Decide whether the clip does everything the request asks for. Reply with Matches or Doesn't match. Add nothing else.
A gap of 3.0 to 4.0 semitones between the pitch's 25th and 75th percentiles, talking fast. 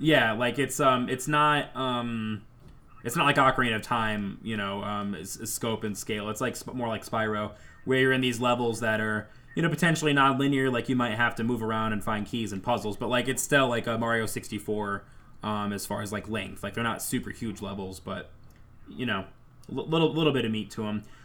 Matches